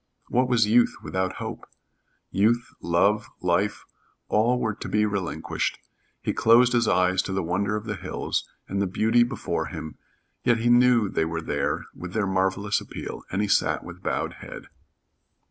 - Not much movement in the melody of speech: No, average, 3.8 semitones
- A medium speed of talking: Yes, average, 170 wpm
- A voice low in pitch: Yes, low, 105 Hz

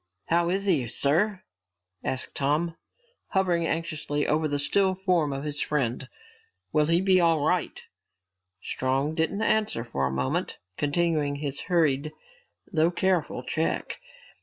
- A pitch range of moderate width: Yes, average, 3.7 semitones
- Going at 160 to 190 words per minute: No, slow, 135 wpm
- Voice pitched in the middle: Yes, medium, 155 Hz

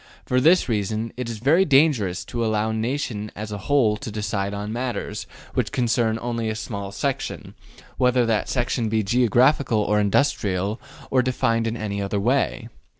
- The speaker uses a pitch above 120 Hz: No, low, 115 Hz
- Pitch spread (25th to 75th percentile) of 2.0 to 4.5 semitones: Yes, average, 3.2 semitones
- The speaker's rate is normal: Yes, average, 170 wpm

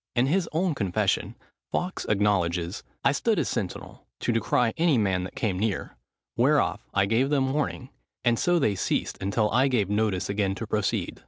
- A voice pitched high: No, low, 110 Hz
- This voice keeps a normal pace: Yes, average, 175 wpm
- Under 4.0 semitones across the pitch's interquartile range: No, average, 5.3 semitones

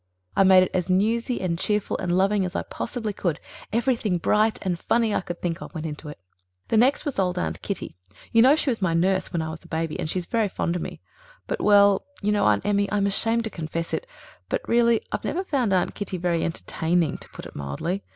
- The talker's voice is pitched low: No, high, 190 Hz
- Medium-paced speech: No, fast, 235 wpm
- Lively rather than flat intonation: No, average, 4.3 semitones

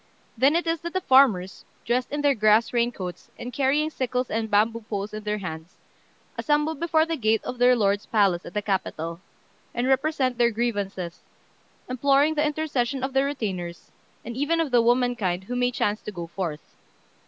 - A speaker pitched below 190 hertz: No, high, 240 Hz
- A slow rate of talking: No, average, 185 wpm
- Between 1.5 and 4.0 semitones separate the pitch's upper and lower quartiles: No, average, 5.1 semitones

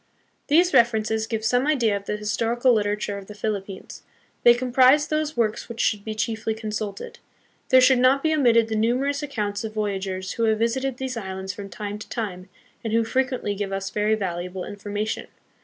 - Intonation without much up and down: No, average, 3.5 semitones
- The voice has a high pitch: Yes, high, 220 Hz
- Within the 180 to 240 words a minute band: Yes, average, 190 wpm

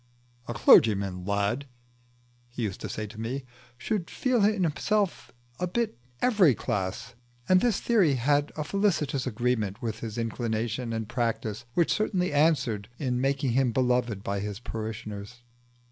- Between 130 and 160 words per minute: Yes, average, 150 wpm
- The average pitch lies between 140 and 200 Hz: No, low, 120 Hz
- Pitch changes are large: Yes, wide, 5.9 semitones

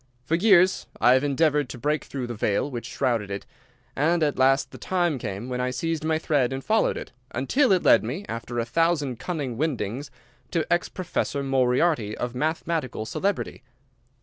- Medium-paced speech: Yes, average, 180 wpm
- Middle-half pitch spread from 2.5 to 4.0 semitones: No, average, 5.1 semitones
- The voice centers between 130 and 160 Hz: Yes, medium, 140 Hz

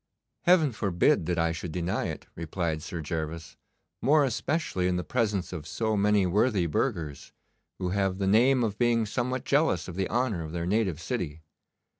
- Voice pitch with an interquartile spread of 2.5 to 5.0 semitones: No, wide, 5.6 semitones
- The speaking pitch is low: Yes, very low, 95 Hz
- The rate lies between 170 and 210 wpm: Yes, average, 175 wpm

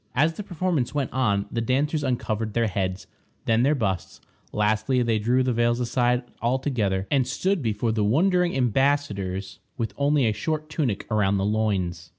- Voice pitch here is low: Yes, low, 120 Hz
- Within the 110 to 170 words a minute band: Yes, average, 165 wpm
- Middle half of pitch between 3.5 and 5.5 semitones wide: Yes, average, 5.0 semitones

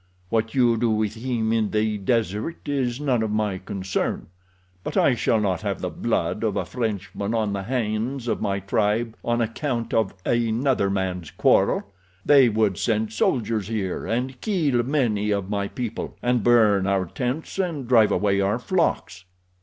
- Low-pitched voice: Yes, low, 110 Hz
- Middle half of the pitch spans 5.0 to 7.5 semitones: No, average, 3.3 semitones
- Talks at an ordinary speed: Yes, average, 165 wpm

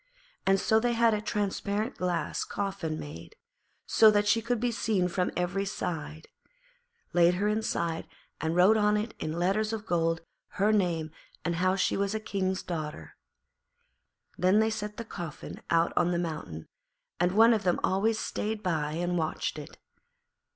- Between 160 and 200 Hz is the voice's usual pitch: Yes, high, 190 Hz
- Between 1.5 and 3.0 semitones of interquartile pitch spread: No, average, 3.9 semitones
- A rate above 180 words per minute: No, average, 165 wpm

